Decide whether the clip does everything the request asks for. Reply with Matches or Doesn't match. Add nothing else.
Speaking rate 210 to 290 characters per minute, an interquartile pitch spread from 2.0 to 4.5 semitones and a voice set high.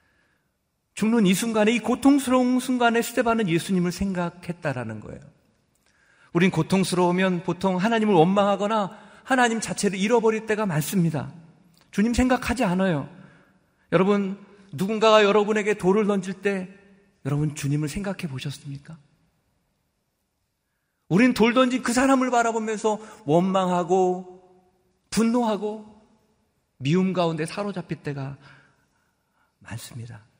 Matches